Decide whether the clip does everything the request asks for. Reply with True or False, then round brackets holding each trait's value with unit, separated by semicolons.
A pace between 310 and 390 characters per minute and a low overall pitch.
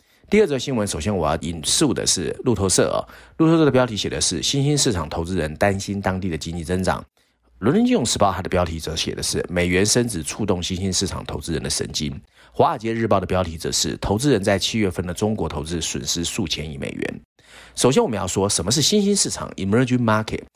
True (375 characters per minute; 95 Hz)